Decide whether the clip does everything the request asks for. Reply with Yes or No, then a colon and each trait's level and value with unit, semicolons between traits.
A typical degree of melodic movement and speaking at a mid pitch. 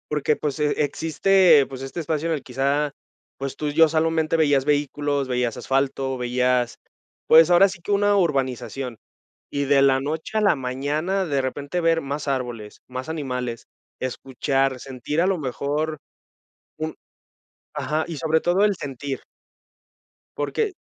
Yes: average, 3.2 semitones; medium, 145 Hz